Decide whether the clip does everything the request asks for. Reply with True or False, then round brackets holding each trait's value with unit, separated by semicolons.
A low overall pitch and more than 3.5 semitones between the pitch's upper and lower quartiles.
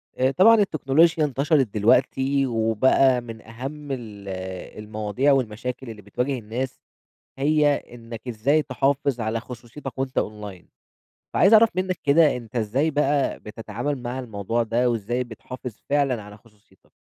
True (125 Hz; 4.0 semitones)